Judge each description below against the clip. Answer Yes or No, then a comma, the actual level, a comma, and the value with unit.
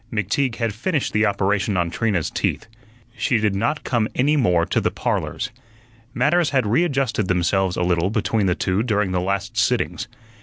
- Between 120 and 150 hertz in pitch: No, low, 105 Hz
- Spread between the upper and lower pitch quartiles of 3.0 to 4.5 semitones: No, average, 4.9 semitones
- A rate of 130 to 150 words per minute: No, average, 175 wpm